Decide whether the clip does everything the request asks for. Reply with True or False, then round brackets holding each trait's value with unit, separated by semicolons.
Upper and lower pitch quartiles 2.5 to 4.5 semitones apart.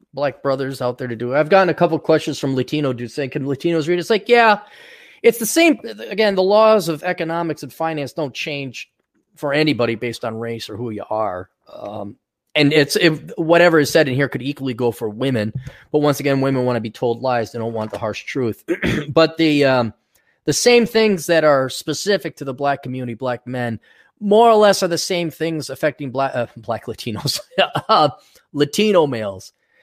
False (5.3 semitones)